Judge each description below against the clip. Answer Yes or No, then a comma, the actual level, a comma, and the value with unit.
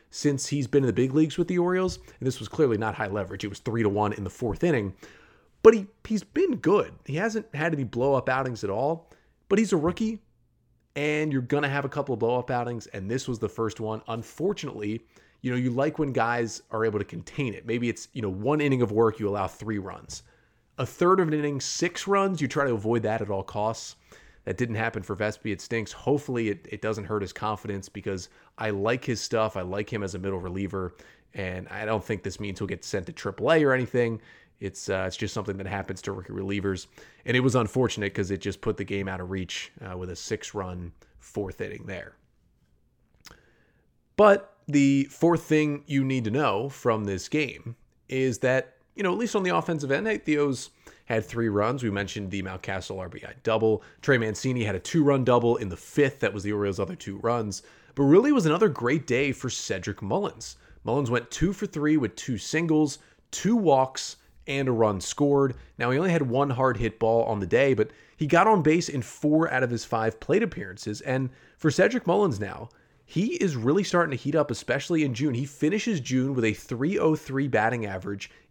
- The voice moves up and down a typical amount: No, wide, 5.7 semitones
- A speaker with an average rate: No, fast, 220 wpm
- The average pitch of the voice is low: Yes, low, 120 Hz